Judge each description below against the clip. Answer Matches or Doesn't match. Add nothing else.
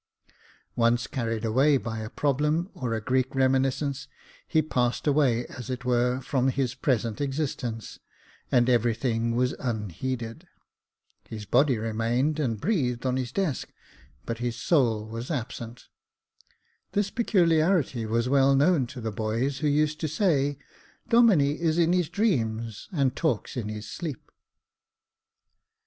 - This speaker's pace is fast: Doesn't match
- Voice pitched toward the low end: Matches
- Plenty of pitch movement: Doesn't match